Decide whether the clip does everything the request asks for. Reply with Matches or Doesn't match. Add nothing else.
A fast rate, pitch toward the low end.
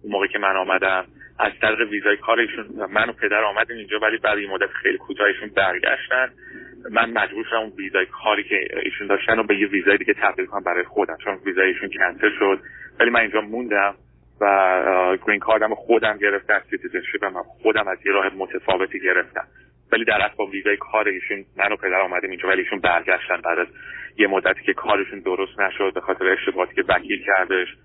Matches